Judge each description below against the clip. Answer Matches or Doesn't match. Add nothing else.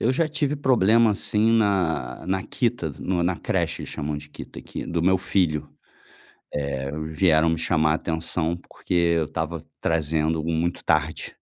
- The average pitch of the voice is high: Doesn't match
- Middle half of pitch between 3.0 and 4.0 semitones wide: Matches